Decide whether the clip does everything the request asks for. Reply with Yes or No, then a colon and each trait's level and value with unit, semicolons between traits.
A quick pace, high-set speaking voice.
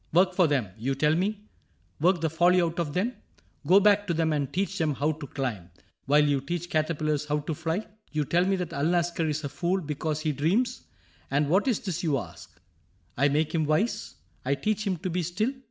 No: fast, 220 wpm; medium, 160 Hz